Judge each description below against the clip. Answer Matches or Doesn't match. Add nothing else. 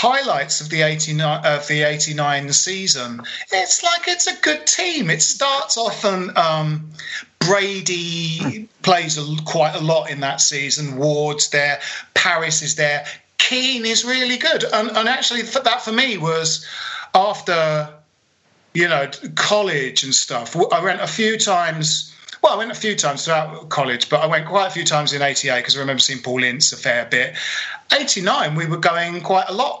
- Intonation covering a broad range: Matches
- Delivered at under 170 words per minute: Doesn't match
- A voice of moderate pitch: Matches